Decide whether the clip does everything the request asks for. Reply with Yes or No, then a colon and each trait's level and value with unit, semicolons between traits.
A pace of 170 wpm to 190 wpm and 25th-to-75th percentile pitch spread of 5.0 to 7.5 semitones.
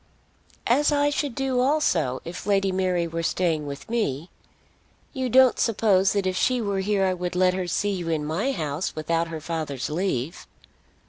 Yes: average, 180 wpm; average, 5.3 semitones